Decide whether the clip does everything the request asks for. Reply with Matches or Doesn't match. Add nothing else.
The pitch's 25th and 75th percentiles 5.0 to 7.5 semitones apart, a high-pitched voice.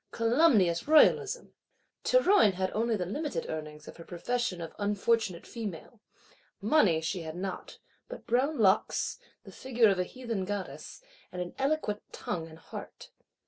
Matches